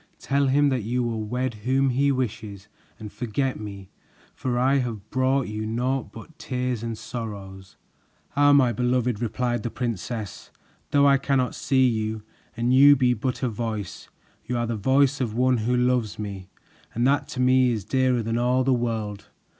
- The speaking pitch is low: Yes, low, 125 Hz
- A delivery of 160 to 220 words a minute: Yes, average, 180 wpm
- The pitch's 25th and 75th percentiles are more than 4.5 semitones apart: No, average, 3.0 semitones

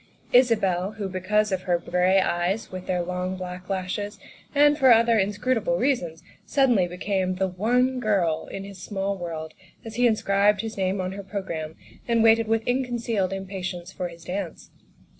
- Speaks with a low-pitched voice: No, high, 195 Hz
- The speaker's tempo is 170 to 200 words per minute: Yes, average, 175 wpm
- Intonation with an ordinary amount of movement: Yes, average, 3.6 semitones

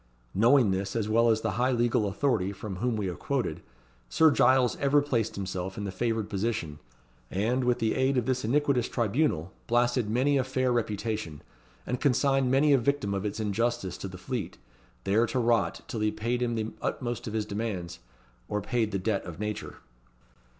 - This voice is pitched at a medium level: No, low, 115 Hz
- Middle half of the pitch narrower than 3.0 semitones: No, average, 3.6 semitones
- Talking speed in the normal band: Yes, average, 190 wpm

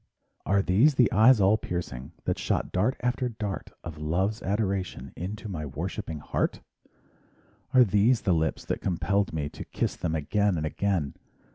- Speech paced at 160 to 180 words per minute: Yes, average, 170 wpm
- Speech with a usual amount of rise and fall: Yes, average, 4.9 semitones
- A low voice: Yes, very low, 95 Hz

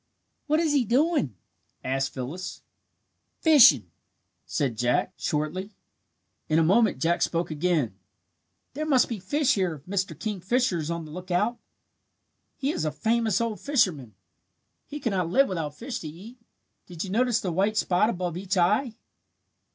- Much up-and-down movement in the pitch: Yes, wide, 6.8 semitones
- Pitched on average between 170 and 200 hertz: Yes, medium, 185 Hz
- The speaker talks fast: No, average, 155 wpm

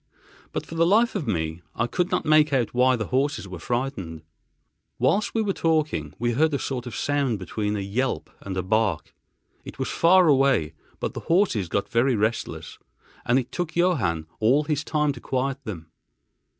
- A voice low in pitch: Yes, low, 130 Hz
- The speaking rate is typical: Yes, average, 190 wpm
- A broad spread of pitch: Yes, wide, 6.7 semitones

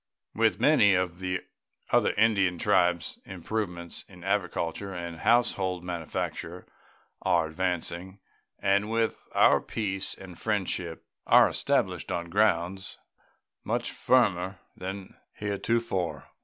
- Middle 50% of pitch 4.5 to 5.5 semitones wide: No, average, 2.7 semitones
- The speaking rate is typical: No, slow, 110 wpm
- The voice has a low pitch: Yes, very low, 95 Hz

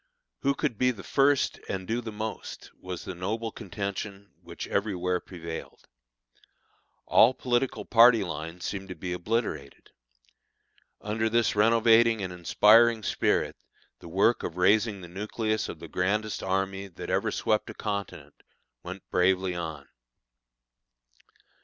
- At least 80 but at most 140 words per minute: Yes, slow, 135 wpm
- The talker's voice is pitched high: No, low, 100 Hz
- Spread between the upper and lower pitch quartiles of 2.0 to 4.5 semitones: Yes, average, 3.7 semitones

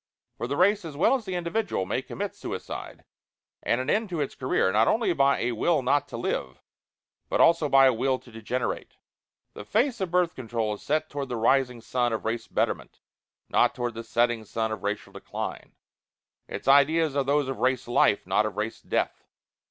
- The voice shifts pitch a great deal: Yes, wide, 5.8 semitones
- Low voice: Yes, low, 130 Hz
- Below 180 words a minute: No, average, 200 wpm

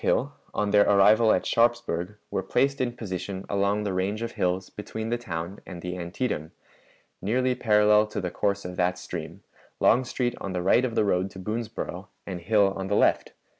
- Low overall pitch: Yes, low, 100 Hz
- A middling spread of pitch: Yes, average, 3.3 semitones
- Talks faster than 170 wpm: Yes, average, 190 wpm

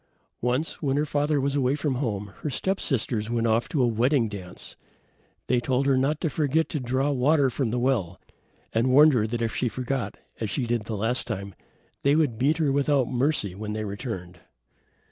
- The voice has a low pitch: Yes, low, 125 Hz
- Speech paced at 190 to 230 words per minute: Yes, average, 200 wpm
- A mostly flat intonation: No, average, 4.1 semitones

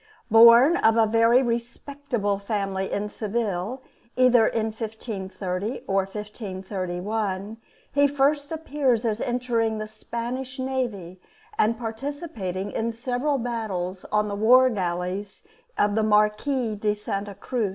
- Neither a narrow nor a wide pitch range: Yes, average, 3.6 semitones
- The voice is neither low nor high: No, high, 220 Hz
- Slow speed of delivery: Yes, slow, 120 wpm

